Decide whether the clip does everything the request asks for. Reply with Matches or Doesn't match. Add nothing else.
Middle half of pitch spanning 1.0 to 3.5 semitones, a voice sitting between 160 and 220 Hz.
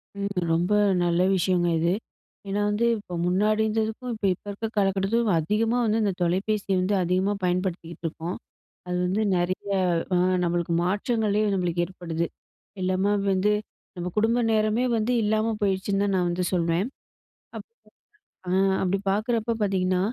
Matches